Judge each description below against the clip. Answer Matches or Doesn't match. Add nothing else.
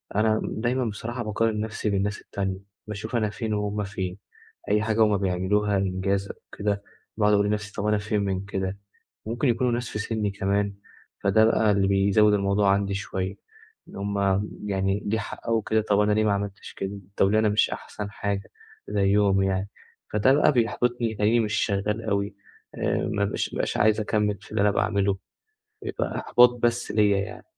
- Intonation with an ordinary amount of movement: Doesn't match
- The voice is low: Matches